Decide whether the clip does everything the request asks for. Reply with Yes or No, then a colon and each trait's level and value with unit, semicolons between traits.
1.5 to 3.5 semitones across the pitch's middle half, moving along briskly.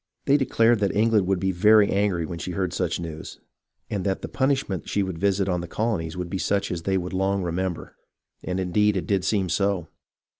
Yes: narrow, 2.4 semitones; fast, 215 wpm